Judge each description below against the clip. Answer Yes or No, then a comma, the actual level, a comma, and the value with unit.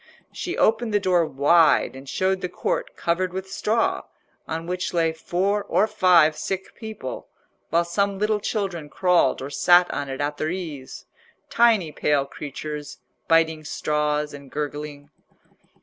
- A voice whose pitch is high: No, medium, 170 Hz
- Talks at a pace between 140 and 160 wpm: Yes, average, 145 wpm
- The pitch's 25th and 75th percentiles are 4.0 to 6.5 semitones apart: Yes, average, 4.4 semitones